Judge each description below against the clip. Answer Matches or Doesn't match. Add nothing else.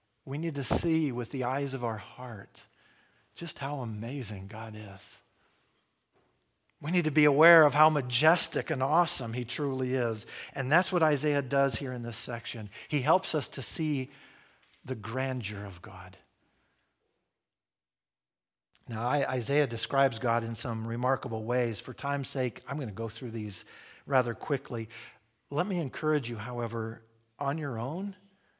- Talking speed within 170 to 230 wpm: Doesn't match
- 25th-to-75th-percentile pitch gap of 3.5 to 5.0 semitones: Matches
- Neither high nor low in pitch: Doesn't match